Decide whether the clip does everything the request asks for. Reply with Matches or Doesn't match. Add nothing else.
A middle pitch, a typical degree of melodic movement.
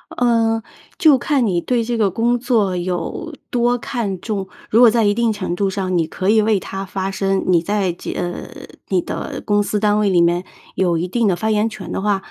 Doesn't match